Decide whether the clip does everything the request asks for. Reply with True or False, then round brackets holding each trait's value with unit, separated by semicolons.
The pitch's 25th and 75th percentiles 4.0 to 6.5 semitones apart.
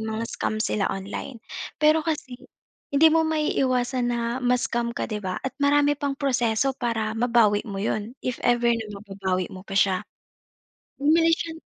True (4.7 semitones)